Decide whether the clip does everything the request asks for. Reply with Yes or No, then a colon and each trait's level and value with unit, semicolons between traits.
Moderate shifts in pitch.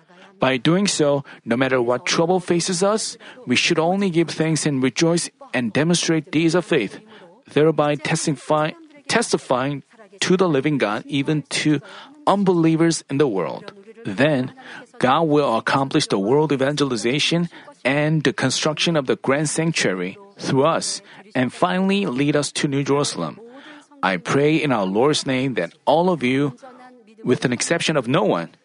Yes: average, 4.5 semitones